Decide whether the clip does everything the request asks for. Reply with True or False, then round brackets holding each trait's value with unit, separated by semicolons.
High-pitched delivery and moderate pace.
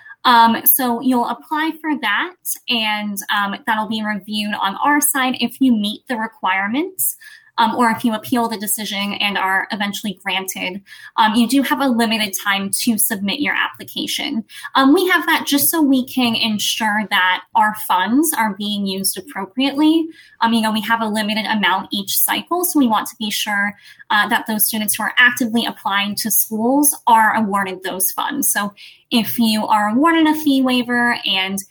True (225 Hz; 180 wpm)